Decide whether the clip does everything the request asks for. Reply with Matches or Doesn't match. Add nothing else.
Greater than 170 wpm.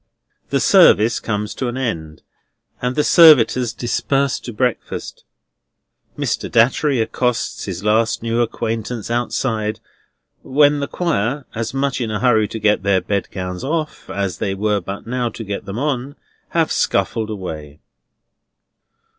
Doesn't match